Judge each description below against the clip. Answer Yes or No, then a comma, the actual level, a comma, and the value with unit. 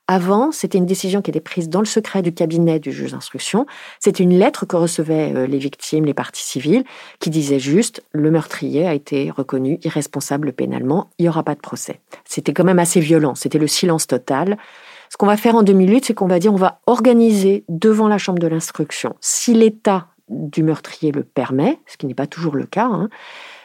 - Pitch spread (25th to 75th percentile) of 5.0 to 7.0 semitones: Yes, average, 5.3 semitones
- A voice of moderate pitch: Yes, medium, 175 Hz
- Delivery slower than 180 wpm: No, average, 210 wpm